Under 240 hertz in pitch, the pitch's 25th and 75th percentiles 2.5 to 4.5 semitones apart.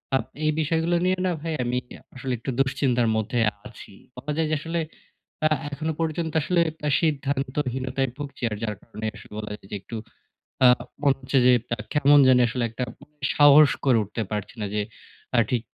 Yes: low, 135 Hz; average, 3.8 semitones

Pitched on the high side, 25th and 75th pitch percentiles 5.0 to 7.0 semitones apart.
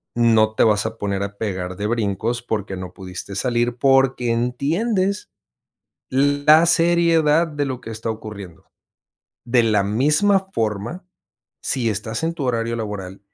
No: low, 115 Hz; average, 5.3 semitones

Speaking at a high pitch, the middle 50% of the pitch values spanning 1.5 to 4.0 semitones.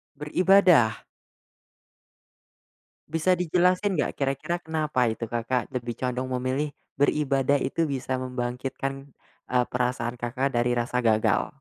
No: low, 130 Hz; average, 3.5 semitones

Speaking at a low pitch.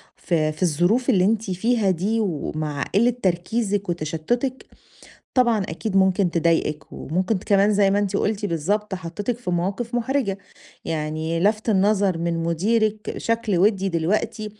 No: high, 195 Hz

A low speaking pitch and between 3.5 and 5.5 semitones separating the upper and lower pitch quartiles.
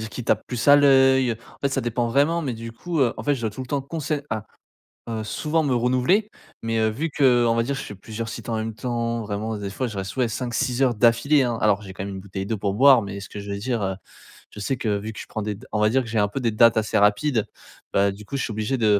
Yes: low, 115 Hz; average, 3.9 semitones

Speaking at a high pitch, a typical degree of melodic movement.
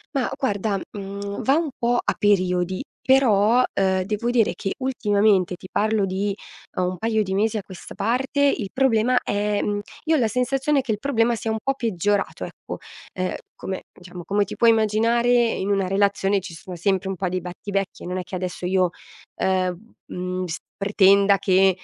Yes: high, 200 Hz; average, 3.3 semitones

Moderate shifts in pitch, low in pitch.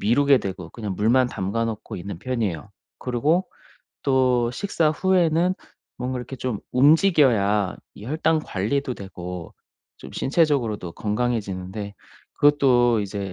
No: wide, 5.8 semitones; low, 120 Hz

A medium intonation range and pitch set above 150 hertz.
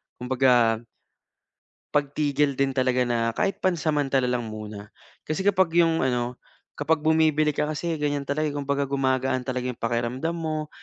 No: average, 3.7 semitones; medium, 140 Hz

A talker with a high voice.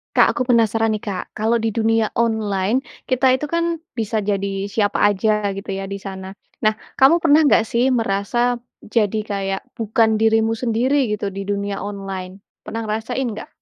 Yes: high, 220 Hz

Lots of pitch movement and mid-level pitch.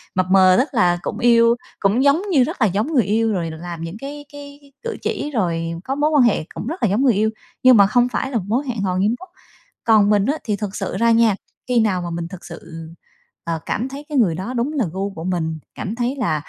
No: wide, 6.1 semitones; high, 220 Hz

